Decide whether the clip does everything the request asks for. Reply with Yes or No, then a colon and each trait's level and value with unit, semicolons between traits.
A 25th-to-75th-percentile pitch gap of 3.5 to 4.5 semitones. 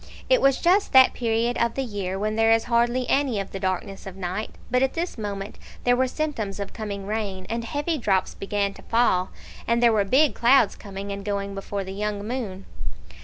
Yes: average, 3.8 semitones